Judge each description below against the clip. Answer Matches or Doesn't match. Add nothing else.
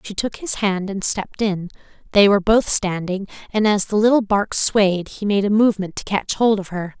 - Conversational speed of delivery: Doesn't match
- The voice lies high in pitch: Matches